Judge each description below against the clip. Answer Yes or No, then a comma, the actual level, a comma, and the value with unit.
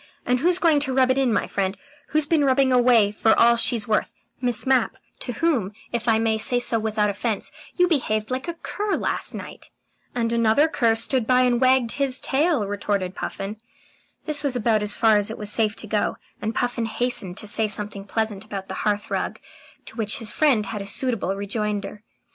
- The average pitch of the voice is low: No, high, 230 Hz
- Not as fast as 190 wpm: No, average, 200 wpm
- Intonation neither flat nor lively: Yes, average, 3.6 semitones